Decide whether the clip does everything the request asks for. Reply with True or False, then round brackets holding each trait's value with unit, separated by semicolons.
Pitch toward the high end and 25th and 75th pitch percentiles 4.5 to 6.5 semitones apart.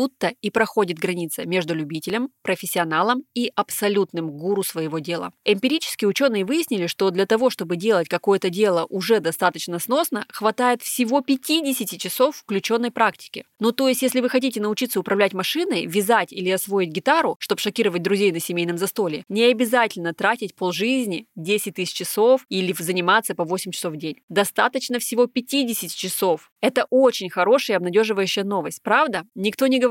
True (205 Hz; 4.8 semitones)